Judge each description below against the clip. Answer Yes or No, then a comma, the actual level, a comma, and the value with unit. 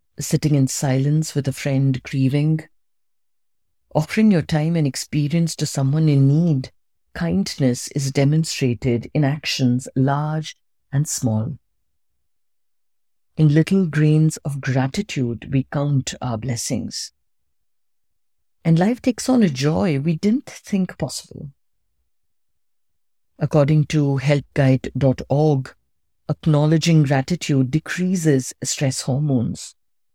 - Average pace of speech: No, slow, 100 wpm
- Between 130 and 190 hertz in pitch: Yes, medium, 140 Hz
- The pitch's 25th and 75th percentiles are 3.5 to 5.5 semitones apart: Yes, average, 4.6 semitones